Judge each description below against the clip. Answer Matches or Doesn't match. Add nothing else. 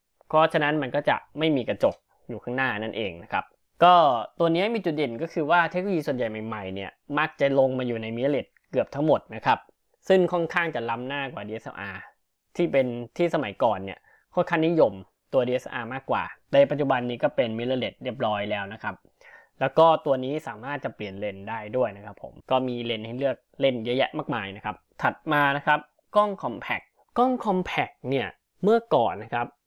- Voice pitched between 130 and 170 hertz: Matches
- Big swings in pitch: Matches